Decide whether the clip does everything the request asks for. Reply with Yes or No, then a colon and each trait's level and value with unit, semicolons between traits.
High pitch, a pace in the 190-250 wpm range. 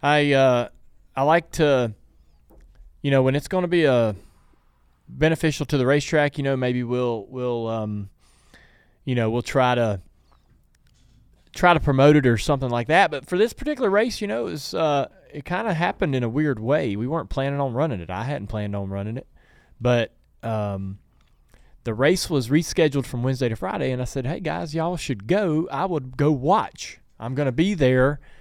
No: low, 135 Hz; average, 195 wpm